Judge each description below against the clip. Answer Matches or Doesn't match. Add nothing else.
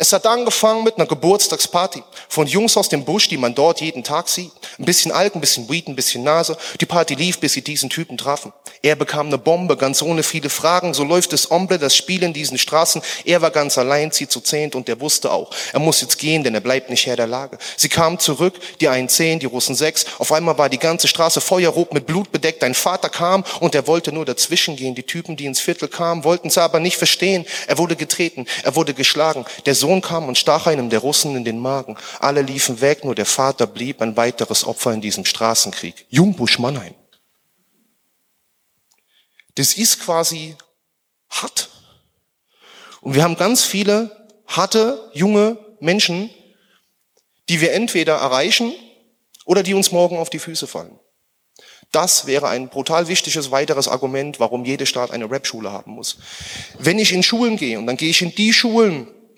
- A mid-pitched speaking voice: Matches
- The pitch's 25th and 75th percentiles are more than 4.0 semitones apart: Matches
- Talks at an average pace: Doesn't match